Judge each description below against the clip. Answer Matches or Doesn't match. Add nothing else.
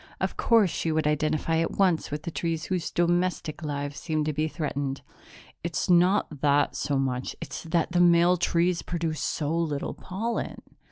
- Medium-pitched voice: Matches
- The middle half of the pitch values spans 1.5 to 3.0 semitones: Matches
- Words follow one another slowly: Doesn't match